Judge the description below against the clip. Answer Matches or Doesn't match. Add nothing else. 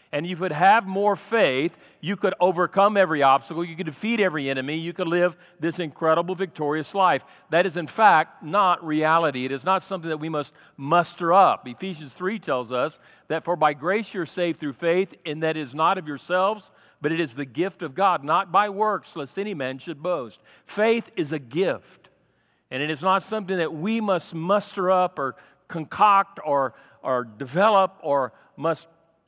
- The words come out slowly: Doesn't match